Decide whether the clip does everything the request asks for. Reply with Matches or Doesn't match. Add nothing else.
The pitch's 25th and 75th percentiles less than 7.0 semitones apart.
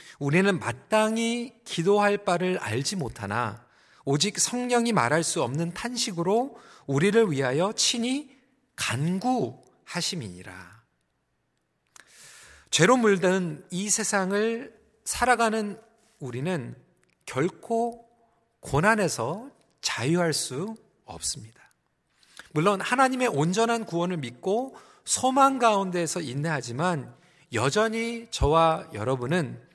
Doesn't match